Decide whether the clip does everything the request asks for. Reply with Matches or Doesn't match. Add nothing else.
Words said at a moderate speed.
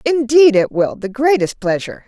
Matches